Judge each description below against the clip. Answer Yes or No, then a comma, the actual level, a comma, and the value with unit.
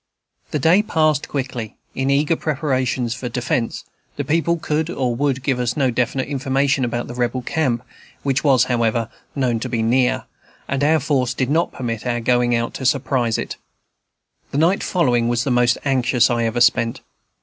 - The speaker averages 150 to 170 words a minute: No, average, 180 wpm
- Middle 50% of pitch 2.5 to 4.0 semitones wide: Yes, average, 2.8 semitones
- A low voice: Yes, low, 130 Hz